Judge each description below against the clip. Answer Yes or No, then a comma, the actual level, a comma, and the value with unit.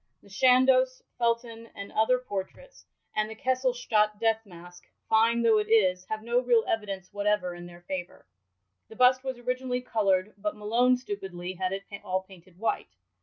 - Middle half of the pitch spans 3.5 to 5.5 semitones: Yes, average, 4.5 semitones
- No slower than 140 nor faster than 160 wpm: No, average, 170 wpm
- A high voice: Yes, high, 220 Hz